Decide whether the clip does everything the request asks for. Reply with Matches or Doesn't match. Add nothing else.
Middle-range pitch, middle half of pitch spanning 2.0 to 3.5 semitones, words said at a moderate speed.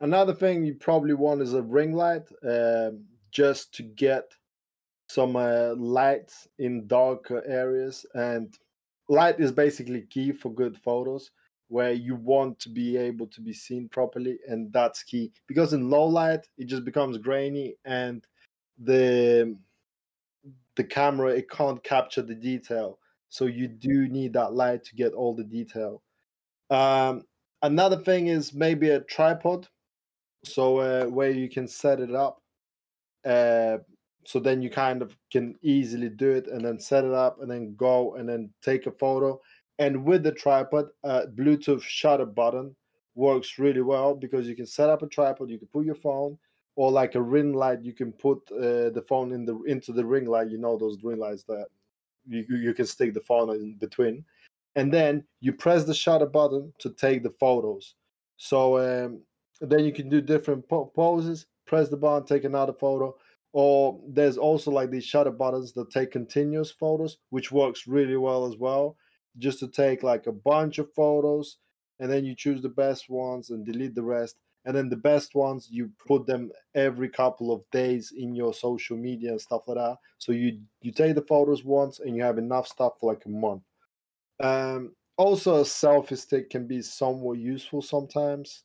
Doesn't match